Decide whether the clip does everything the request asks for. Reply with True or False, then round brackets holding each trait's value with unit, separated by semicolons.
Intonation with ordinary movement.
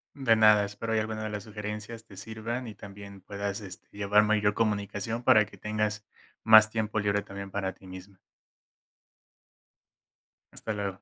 False (1.4 semitones)